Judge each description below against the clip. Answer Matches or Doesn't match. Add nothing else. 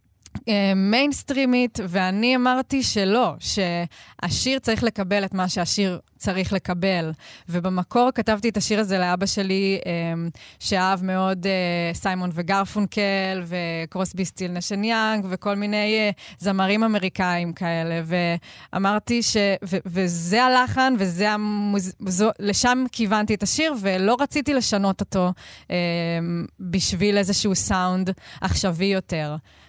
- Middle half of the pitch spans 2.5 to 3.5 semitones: Matches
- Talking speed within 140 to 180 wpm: Doesn't match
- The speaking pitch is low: Doesn't match